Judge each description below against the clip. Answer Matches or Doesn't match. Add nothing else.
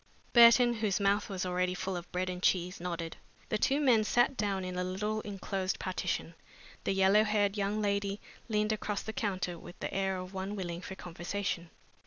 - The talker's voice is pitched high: Matches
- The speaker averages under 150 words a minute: Doesn't match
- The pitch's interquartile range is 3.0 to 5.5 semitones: Doesn't match